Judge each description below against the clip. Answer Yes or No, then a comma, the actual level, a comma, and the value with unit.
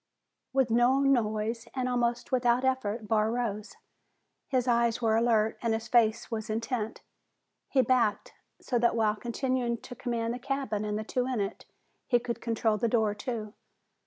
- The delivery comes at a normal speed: Yes, average, 165 wpm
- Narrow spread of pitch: Yes, narrow, 2.1 semitones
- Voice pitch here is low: No, high, 235 Hz